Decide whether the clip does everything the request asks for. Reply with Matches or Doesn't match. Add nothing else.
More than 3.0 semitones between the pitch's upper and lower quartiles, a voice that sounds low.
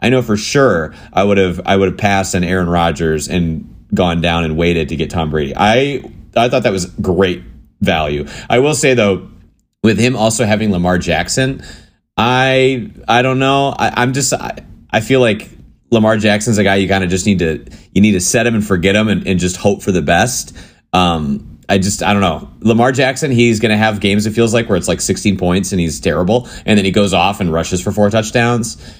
Matches